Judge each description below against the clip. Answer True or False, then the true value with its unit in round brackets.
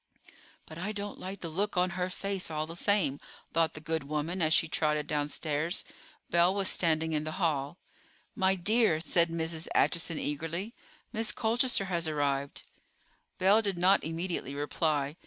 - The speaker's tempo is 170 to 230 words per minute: False (160 wpm)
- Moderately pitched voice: True (165 Hz)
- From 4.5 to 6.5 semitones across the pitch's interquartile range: False (3.5 semitones)